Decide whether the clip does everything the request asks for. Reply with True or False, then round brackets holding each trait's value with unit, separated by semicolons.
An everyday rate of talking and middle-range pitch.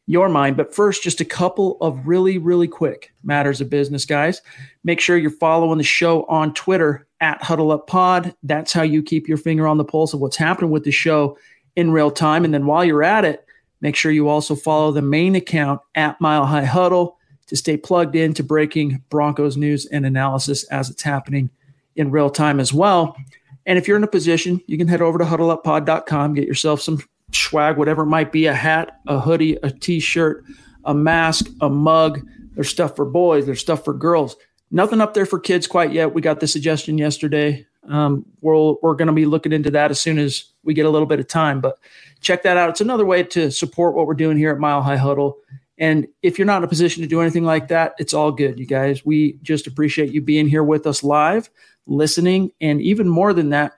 False (220 wpm; 155 Hz)